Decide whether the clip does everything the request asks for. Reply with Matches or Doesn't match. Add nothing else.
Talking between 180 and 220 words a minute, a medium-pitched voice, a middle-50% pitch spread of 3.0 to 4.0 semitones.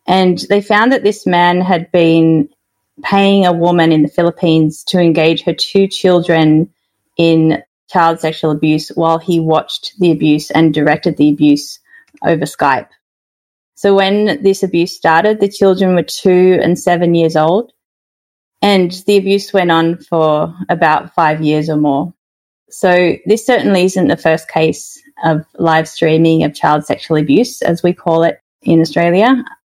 Doesn't match